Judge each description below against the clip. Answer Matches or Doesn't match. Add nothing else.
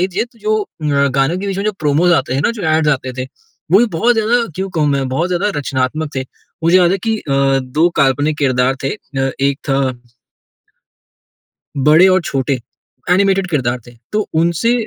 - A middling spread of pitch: Doesn't match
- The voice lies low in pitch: Doesn't match